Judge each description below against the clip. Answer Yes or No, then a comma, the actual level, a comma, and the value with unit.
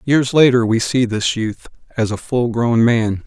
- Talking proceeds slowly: No, average, 200 wpm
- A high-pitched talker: No, low, 120 Hz